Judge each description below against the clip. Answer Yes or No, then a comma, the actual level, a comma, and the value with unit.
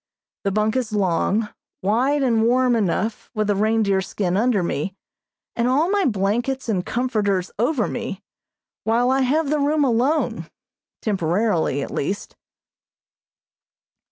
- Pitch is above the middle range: Yes, high, 225 Hz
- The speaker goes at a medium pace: No, slow, 130 wpm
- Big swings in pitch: No, average, 4.5 semitones